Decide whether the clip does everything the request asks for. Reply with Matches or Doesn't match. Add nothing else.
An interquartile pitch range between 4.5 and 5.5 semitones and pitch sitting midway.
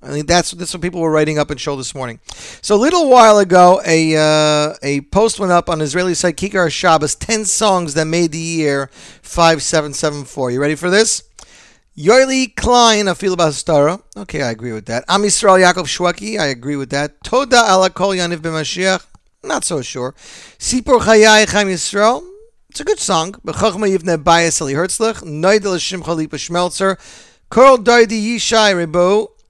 Matches